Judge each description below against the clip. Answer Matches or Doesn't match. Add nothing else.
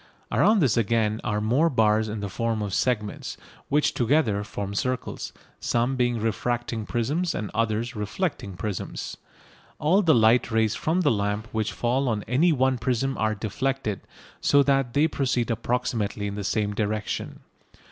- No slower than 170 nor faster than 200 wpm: Doesn't match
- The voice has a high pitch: Doesn't match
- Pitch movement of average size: Matches